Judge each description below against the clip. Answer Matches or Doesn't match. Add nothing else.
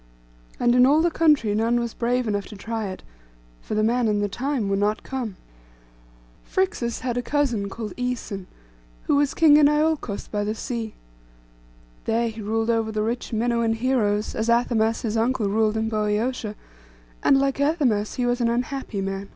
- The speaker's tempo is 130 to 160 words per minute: Doesn't match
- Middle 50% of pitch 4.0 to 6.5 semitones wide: Doesn't match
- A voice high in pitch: Matches